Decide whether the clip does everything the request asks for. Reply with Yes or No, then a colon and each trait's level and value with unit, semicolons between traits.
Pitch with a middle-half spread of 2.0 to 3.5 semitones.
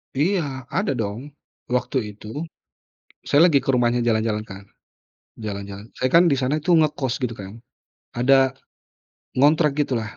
No: average, 4.8 semitones